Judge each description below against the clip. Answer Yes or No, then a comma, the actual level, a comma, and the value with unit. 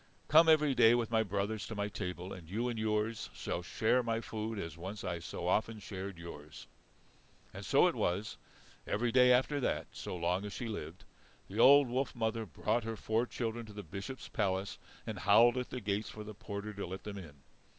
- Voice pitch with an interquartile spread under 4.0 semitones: Yes, average, 3.4 semitones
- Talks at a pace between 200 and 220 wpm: Yes, fast, 205 wpm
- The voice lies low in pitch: Yes, low, 105 Hz